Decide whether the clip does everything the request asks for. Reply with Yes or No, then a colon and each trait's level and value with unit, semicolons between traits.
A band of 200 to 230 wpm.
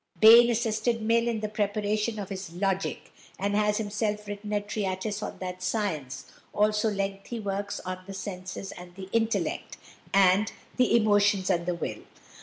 No: average, 160 wpm